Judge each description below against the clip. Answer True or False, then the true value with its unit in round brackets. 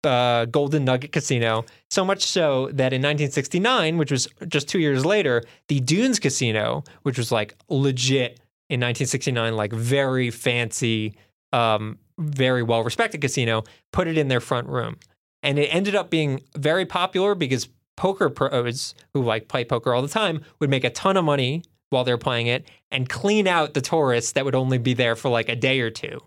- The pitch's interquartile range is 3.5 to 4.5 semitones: True (4.2 semitones)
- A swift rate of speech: False (185 wpm)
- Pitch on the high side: False (130 Hz)